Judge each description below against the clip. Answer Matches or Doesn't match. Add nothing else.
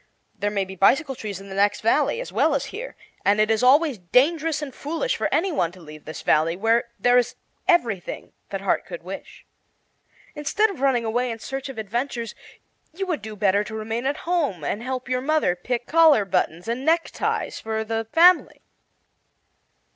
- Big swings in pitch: Matches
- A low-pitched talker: Doesn't match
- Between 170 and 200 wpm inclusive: Matches